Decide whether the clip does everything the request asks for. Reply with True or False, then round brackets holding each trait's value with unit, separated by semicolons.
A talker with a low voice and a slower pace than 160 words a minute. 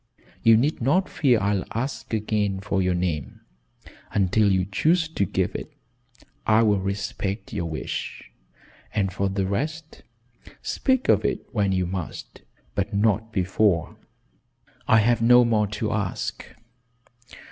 True (105 Hz; 135 wpm)